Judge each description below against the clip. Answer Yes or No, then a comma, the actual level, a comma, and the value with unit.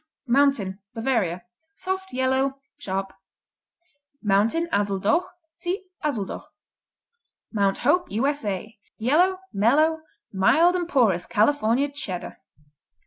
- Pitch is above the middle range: Yes, high, 245 Hz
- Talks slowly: Yes, slow, 85 wpm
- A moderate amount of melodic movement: No, wide, 6.9 semitones